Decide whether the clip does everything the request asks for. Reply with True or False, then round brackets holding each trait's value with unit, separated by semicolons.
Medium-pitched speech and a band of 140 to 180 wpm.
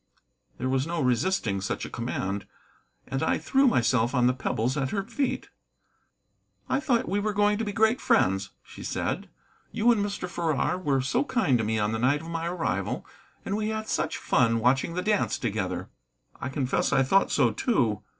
False (145 Hz; 190 wpm)